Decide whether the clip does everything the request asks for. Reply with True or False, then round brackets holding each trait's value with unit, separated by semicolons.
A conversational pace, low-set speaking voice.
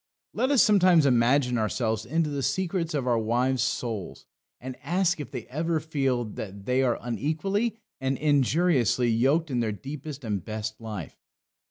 True (160 wpm; 130 Hz)